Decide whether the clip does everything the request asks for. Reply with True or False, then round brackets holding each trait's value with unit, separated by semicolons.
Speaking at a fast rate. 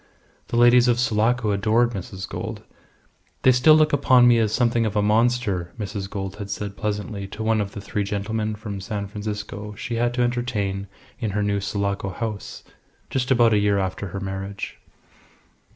False (180 wpm)